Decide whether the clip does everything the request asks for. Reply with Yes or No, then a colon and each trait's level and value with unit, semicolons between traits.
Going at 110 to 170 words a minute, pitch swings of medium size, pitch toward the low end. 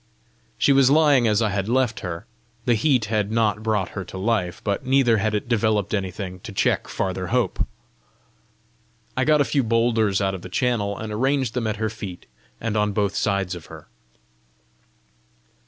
No: average, 180 wpm; average, 3.5 semitones; low, 110 Hz